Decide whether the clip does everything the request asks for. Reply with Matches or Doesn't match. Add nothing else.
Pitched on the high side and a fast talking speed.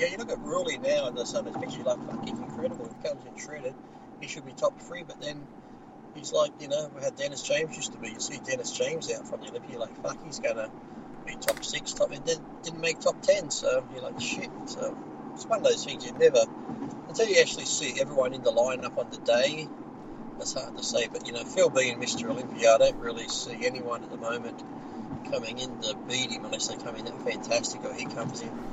Matches